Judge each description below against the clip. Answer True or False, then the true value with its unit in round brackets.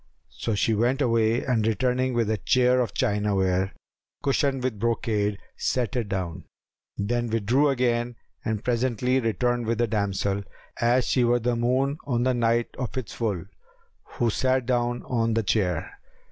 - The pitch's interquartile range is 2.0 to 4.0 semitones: True (2.7 semitones)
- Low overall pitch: True (120 Hz)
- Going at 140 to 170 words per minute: True (160 wpm)